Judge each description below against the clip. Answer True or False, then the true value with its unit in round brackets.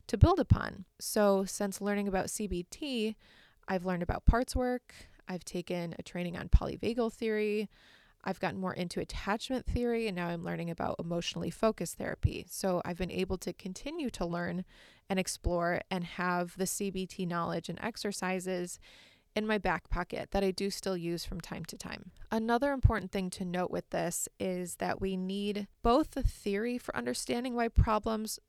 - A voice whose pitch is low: False (190 Hz)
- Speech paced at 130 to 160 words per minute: False (175 wpm)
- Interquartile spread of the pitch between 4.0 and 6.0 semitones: False (3.2 semitones)